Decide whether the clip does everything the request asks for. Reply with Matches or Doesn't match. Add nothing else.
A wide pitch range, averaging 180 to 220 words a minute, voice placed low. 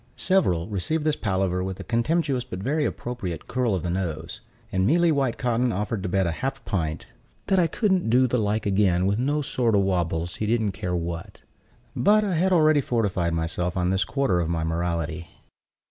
Matches